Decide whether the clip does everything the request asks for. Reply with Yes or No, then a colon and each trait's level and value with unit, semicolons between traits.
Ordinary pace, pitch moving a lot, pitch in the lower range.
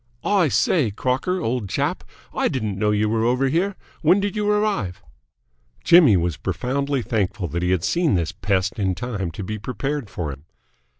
Yes: average, 180 wpm; wide, 7.6 semitones; low, 115 Hz